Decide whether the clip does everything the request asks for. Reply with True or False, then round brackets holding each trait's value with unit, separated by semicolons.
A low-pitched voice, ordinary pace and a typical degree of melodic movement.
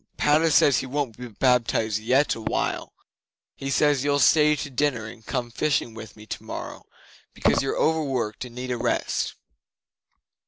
True (130 Hz; 160 wpm; 4.0 semitones)